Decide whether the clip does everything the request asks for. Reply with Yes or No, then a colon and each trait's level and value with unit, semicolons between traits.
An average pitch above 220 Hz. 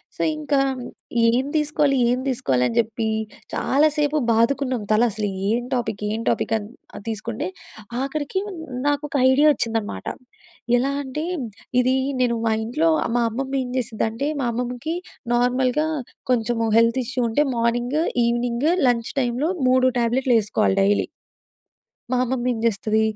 Yes: high, 245 Hz